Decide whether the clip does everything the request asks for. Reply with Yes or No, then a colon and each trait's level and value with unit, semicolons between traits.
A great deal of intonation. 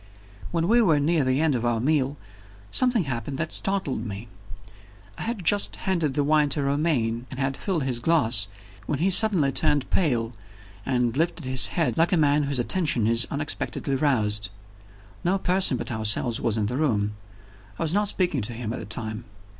Yes: wide, 5.8 semitones